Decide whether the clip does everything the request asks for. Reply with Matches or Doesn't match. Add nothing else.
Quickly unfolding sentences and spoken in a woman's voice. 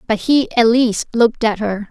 Matches